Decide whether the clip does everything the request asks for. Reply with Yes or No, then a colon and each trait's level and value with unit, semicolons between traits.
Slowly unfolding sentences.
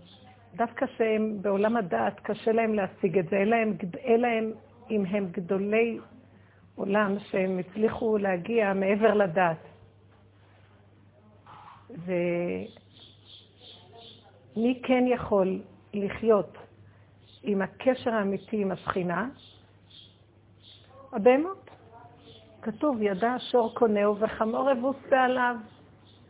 Yes: slow, 85 wpm